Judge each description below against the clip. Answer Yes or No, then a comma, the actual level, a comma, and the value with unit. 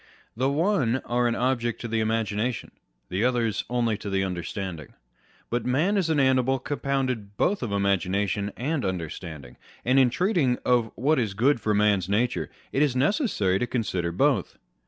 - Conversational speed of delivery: Yes, average, 175 wpm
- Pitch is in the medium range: No, low, 120 Hz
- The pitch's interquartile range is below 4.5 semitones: No, average, 4.8 semitones